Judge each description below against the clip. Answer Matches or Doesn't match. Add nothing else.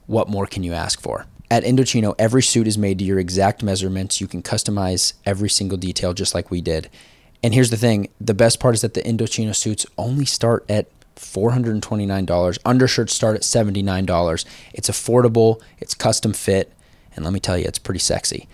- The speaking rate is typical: Matches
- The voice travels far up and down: Doesn't match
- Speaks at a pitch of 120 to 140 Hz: Doesn't match